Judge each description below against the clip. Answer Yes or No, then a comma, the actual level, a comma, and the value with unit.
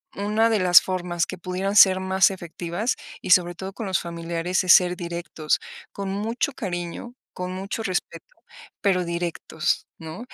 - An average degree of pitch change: No, narrow, 2.2 semitones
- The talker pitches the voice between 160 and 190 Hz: Yes, medium, 185 Hz